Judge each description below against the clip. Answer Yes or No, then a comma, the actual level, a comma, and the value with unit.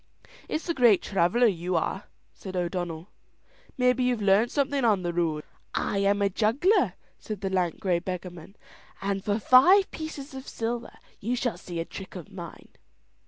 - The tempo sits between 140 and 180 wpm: Yes, average, 165 wpm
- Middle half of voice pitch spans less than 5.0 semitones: No, wide, 5.6 semitones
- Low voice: No, high, 200 Hz